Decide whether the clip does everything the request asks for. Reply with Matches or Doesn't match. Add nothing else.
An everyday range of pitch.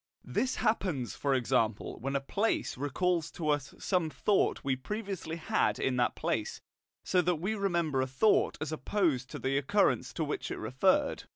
Doesn't match